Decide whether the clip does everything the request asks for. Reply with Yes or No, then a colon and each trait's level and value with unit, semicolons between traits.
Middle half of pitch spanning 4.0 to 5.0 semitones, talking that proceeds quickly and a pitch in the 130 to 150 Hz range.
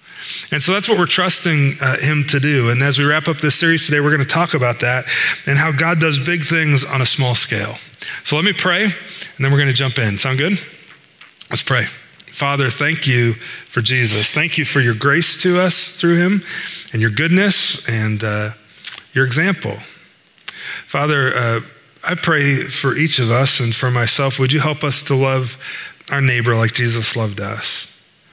No: average, 4.5 semitones; average, 195 wpm; medium, 140 Hz